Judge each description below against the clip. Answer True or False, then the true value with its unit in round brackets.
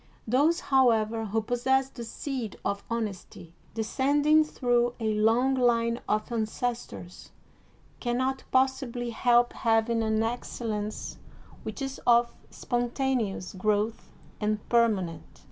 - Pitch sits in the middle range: False (235 Hz)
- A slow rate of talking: True (115 wpm)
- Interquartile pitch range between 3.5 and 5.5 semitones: False (2.8 semitones)